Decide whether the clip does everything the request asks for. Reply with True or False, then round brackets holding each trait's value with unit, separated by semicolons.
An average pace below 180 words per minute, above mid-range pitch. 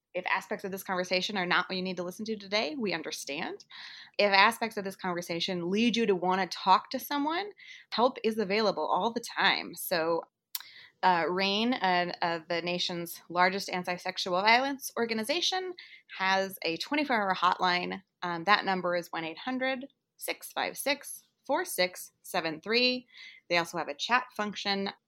True (160 wpm; 195 Hz)